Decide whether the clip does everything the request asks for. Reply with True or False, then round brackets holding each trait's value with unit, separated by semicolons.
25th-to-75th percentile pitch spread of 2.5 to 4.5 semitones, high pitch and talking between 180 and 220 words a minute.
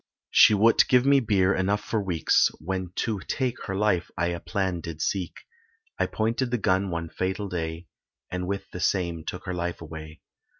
False (3.3 semitones; 95 Hz; 185 wpm)